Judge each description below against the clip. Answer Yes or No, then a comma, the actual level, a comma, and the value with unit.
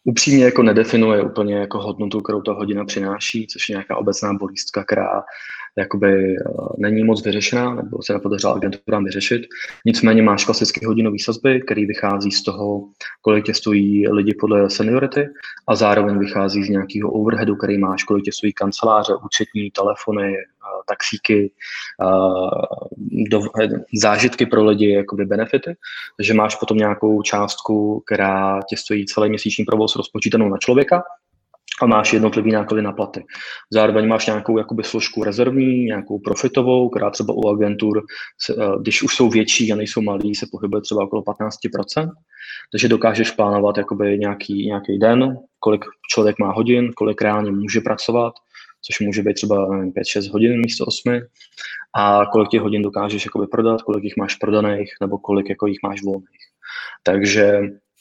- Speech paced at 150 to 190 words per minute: Yes, average, 155 wpm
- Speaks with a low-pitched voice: Yes, low, 105 Hz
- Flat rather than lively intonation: Yes, narrow, 1.6 semitones